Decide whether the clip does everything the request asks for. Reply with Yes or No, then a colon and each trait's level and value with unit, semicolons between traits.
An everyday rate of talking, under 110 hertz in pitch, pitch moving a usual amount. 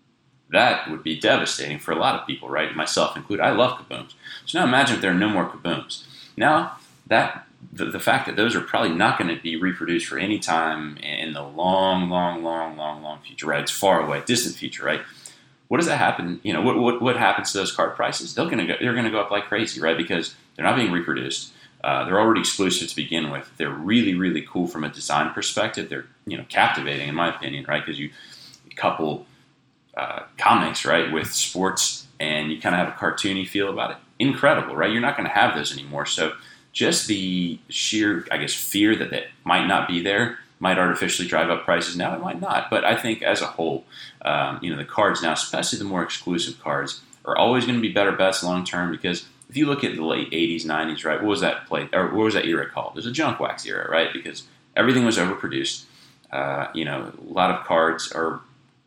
No: fast, 225 wpm; very low, 90 Hz; average, 4.5 semitones